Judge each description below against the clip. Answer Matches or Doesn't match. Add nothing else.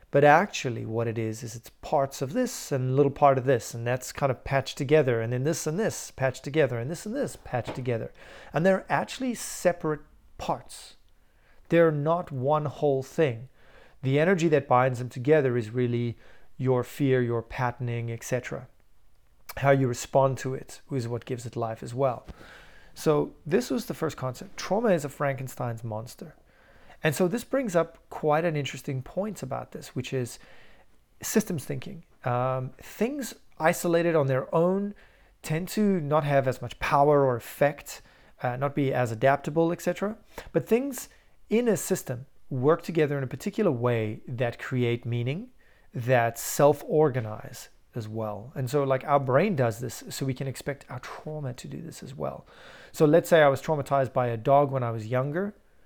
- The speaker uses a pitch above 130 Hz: Matches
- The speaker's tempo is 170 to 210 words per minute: Matches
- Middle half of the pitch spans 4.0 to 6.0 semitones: Matches